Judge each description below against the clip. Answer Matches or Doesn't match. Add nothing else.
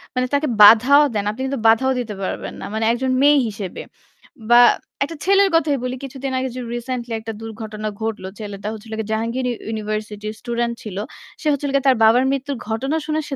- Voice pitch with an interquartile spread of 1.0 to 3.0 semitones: Doesn't match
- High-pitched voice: Matches